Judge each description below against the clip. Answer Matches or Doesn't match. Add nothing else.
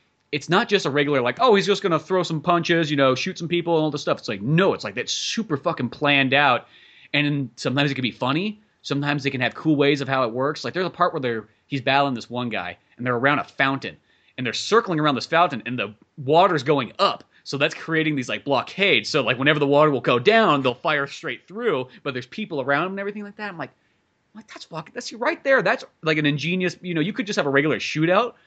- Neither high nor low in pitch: Matches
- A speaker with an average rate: Doesn't match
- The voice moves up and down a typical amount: Matches